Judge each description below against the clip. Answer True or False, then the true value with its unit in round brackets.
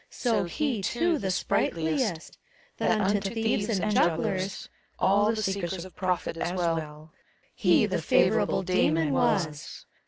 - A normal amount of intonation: True (4.1 semitones)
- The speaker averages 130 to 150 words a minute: True (145 wpm)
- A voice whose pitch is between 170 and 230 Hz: True (190 Hz)